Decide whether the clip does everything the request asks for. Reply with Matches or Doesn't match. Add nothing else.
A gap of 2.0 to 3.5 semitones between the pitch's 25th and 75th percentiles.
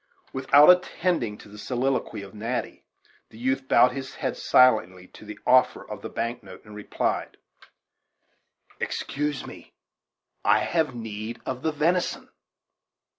Doesn't match